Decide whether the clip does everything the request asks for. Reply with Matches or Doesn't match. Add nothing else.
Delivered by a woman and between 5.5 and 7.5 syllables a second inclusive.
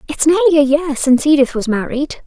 Matches